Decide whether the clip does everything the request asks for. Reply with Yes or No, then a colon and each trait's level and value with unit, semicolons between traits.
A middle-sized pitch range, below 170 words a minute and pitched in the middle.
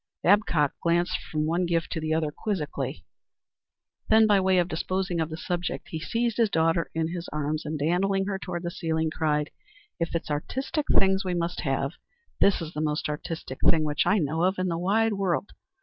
No: average, 3.4 semitones; average, 195 wpm; medium, 170 Hz